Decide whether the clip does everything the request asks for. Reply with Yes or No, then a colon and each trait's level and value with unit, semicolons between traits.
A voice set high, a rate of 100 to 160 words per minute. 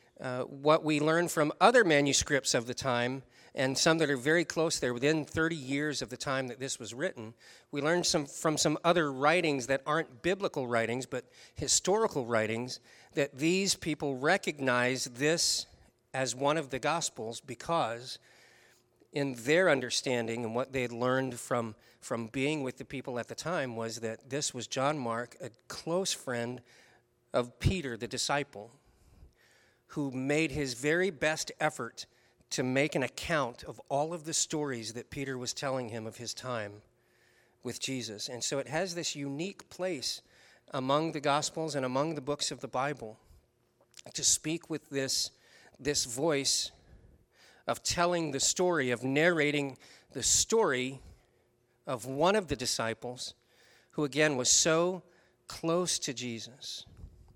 No: low, 135 Hz; average, 155 wpm